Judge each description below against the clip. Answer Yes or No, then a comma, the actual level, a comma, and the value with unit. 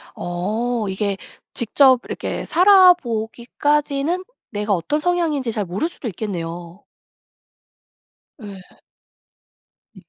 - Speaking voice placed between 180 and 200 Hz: No, high, 230 Hz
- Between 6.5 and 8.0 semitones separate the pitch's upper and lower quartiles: Yes, wide, 7.0 semitones